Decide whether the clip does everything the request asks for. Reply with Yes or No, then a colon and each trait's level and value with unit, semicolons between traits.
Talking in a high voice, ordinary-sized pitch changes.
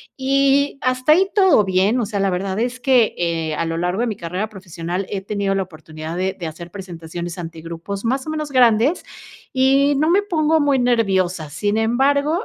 No: high, 205 Hz; wide, 7.4 semitones